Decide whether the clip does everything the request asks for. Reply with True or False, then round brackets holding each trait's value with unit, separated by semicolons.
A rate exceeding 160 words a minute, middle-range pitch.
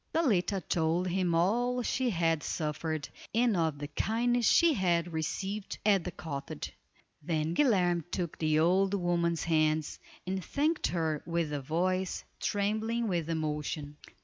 False (140 wpm; 175 Hz)